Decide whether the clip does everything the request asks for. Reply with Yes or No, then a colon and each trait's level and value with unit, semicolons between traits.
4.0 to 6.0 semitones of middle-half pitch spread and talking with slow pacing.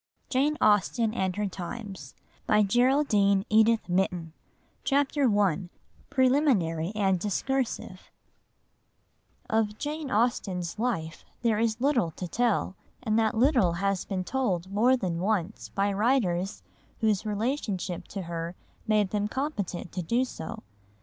Yes: average, 4.7 semitones; slow, 115 wpm